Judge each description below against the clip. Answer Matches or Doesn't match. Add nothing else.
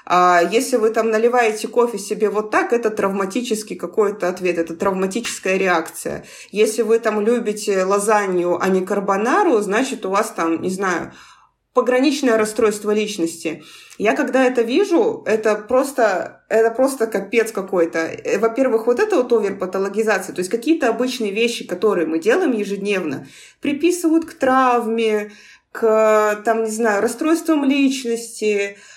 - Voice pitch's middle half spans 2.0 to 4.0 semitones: Matches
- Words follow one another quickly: Doesn't match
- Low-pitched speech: Doesn't match